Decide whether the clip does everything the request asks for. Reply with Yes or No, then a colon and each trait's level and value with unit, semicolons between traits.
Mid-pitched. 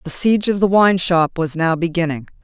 Yes: medium, 175 Hz